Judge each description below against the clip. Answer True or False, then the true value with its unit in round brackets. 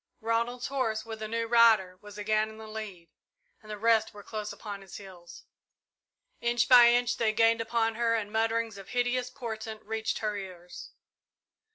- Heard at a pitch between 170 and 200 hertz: False (220 Hz)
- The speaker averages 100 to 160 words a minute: False (175 wpm)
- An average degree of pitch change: False (1.7 semitones)